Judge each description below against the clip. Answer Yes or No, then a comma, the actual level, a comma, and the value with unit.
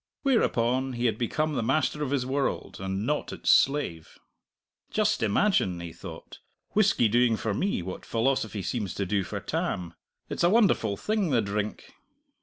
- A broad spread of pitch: Yes, wide, 6.8 semitones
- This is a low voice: Yes, low, 120 Hz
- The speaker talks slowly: No, average, 165 wpm